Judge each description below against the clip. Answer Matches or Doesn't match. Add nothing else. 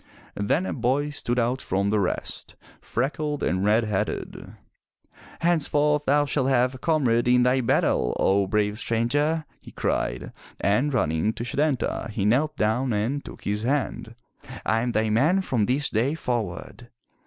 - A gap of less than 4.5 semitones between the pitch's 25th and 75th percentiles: Doesn't match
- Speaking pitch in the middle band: Doesn't match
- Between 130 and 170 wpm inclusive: Matches